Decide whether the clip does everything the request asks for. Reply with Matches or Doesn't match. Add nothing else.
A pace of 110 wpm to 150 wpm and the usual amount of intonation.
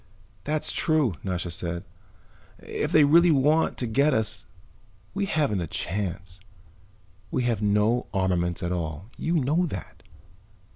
Doesn't match